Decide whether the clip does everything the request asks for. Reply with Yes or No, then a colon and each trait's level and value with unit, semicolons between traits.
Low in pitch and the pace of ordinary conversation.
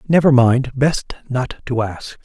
Yes: low, 130 Hz; average, 160 wpm